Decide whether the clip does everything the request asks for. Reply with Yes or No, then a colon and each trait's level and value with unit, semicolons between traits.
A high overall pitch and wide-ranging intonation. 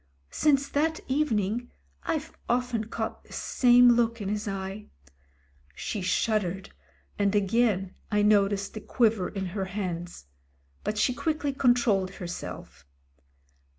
No: high, 210 Hz; average, 4.0 semitones